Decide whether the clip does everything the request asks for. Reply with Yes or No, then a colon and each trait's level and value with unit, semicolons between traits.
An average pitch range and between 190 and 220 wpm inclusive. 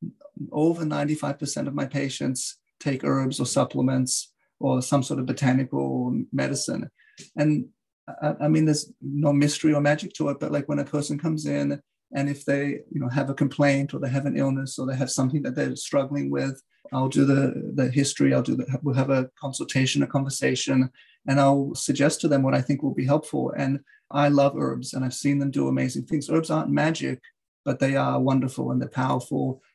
No: narrow, 1.7 semitones; average, 200 wpm